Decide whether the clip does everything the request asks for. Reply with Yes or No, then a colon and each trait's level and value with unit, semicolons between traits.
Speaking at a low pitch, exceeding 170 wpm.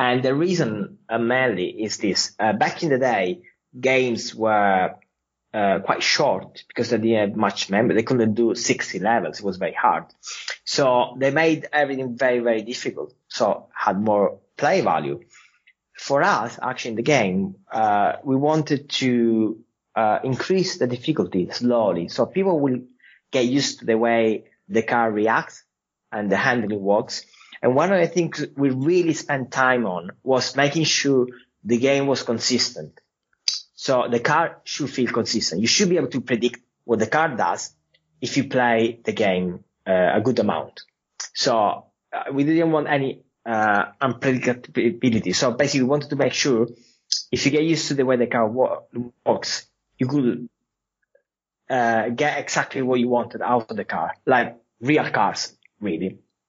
No: low, 125 Hz; average, 165 wpm